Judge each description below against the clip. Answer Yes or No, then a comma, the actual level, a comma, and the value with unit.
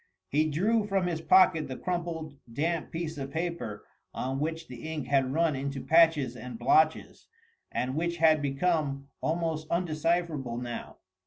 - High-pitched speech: No, medium, 155 Hz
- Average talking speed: Yes, average, 150 wpm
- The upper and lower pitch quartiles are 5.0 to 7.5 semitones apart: No, average, 3.6 semitones